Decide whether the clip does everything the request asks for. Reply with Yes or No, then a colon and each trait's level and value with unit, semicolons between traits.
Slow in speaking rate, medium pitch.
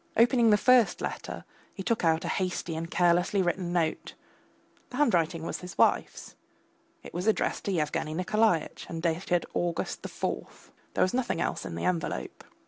No: average, 170 wpm; medium, 180 Hz